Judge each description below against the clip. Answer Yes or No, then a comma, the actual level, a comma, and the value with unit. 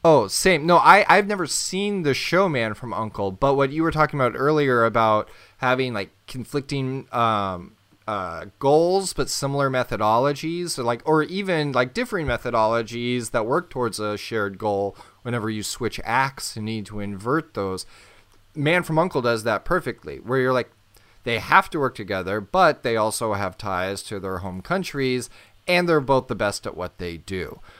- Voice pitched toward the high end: No, low, 125 Hz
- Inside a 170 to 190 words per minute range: Yes, average, 180 wpm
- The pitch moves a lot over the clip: Yes, wide, 6.0 semitones